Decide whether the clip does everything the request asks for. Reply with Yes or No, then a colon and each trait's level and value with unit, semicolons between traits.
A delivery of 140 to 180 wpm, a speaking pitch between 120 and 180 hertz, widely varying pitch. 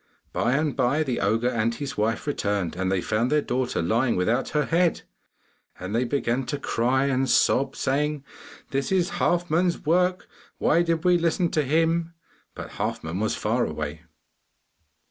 Yes: average, 160 wpm; low, 135 Hz; wide, 5.9 semitones